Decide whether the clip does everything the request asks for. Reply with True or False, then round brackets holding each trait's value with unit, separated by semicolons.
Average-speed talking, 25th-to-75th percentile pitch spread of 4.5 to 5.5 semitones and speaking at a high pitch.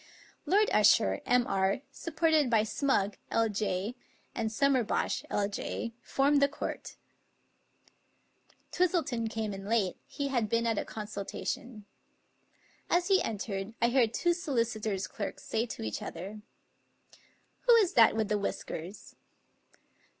False (130 wpm; 5.2 semitones; 225 Hz)